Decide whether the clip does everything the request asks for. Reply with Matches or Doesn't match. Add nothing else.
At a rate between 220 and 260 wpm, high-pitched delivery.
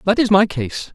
Matches